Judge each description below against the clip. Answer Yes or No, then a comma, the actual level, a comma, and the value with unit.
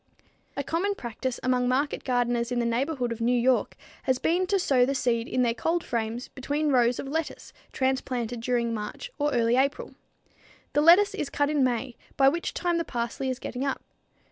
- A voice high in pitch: Yes, very high, 255 Hz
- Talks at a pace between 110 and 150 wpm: No, average, 195 wpm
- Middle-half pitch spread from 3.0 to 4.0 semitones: Yes, average, 3.3 semitones